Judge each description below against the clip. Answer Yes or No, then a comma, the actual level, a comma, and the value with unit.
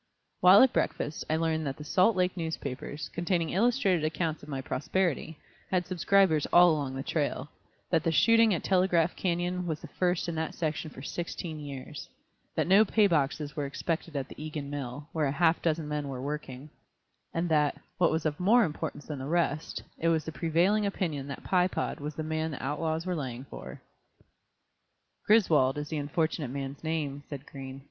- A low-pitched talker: No, medium, 160 Hz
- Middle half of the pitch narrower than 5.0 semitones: Yes, average, 3.3 semitones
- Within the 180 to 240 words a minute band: Yes, average, 190 wpm